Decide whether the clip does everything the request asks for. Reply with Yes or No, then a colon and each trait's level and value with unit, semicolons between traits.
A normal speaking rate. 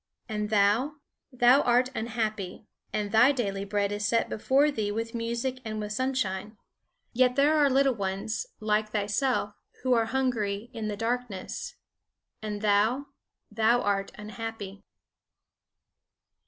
No: slow, 130 wpm